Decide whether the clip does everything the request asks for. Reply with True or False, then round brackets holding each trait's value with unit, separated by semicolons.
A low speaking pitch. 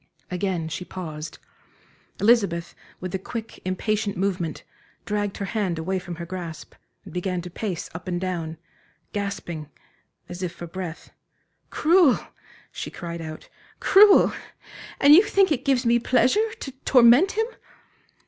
False (190 Hz)